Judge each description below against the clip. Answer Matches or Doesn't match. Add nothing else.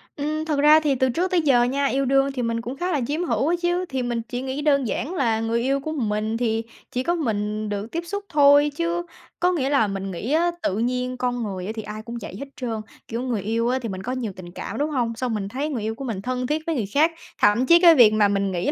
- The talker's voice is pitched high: Matches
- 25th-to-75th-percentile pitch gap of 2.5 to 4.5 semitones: Doesn't match